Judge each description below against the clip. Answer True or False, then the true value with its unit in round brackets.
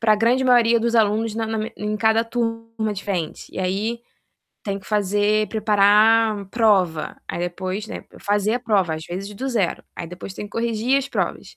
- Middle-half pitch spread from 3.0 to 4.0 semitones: False (2.4 semitones)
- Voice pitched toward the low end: False (215 Hz)